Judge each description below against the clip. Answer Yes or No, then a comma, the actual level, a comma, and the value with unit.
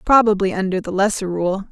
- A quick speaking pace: No, average, 175 wpm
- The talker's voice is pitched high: Yes, high, 195 Hz